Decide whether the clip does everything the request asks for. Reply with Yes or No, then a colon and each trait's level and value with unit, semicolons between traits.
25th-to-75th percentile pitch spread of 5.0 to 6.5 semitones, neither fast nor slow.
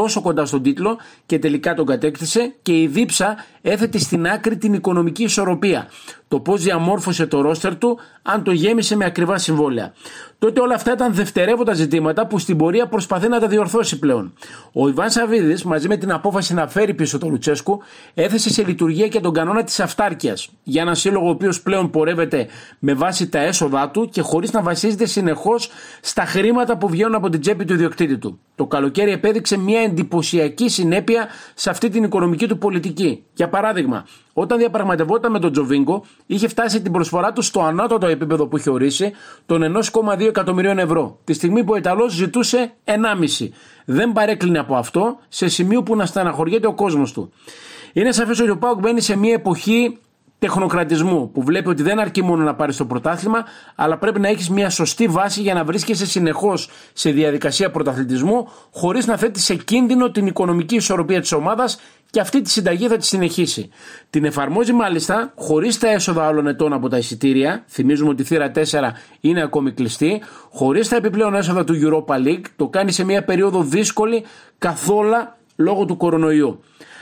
No: wide, 5.5 semitones; fast, 180 wpm